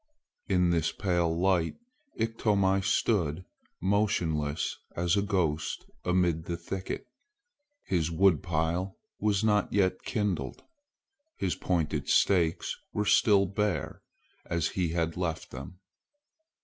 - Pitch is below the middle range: Yes, very low, 90 Hz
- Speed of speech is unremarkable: No, slow, 110 wpm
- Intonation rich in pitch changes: No, average, 3.1 semitones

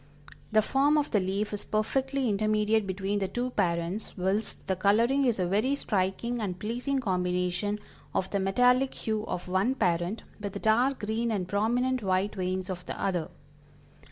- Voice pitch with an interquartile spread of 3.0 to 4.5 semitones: Yes, average, 4.1 semitones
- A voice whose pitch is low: No, high, 210 Hz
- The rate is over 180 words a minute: No, average, 170 wpm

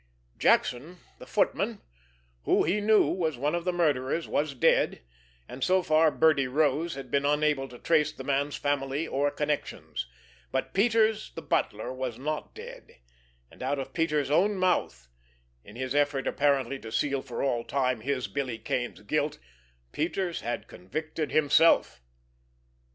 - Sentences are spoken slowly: No, average, 150 wpm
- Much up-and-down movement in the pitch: No, average, 3.5 semitones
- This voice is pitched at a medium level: Yes, medium, 145 Hz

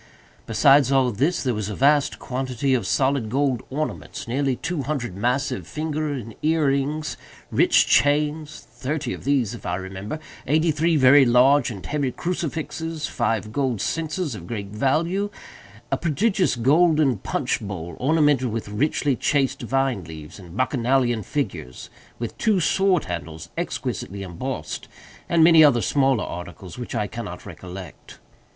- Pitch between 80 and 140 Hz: Yes, low, 135 Hz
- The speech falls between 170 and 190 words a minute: No, average, 145 wpm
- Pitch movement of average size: No, wide, 5.7 semitones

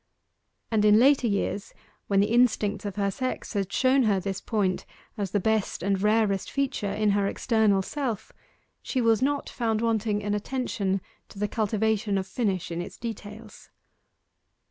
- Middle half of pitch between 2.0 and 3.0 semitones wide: Yes, narrow, 2.4 semitones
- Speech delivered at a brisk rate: No, average, 165 wpm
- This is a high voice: Yes, high, 210 Hz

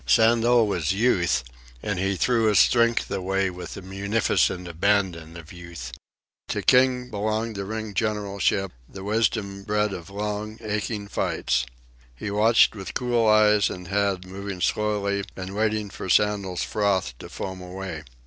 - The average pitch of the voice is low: Yes, low, 100 Hz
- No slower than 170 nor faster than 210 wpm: No, average, 150 wpm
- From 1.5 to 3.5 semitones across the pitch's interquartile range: Yes, narrow, 2.4 semitones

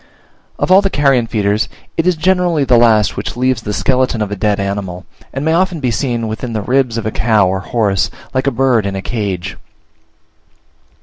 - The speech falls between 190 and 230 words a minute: Yes, average, 200 wpm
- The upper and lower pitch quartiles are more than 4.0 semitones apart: Yes, average, 4.6 semitones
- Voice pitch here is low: Yes, low, 115 Hz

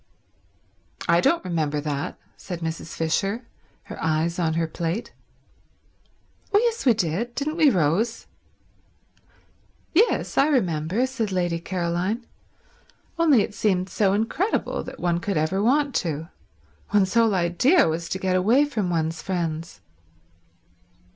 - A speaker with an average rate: No, slow, 125 wpm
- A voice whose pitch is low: No, medium, 185 Hz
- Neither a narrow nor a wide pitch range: No, wide, 5.9 semitones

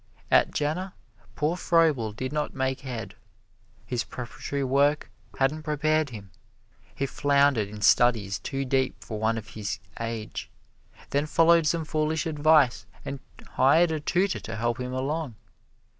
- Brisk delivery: No, average, 145 wpm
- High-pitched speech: No, low, 135 Hz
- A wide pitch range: No, average, 4.8 semitones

